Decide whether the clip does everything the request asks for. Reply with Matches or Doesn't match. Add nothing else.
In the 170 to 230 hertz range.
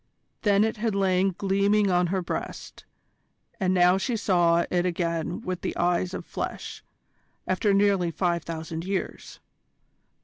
Matches